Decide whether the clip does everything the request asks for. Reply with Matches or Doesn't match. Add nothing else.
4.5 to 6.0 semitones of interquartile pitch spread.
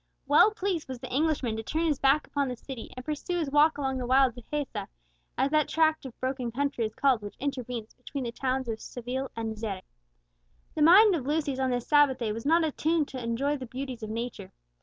Doesn't match